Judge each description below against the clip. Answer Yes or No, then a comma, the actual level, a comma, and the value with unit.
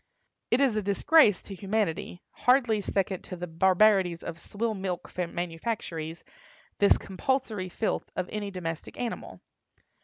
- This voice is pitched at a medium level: No, high, 195 Hz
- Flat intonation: No, average, 3.4 semitones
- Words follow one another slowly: Yes, slow, 130 wpm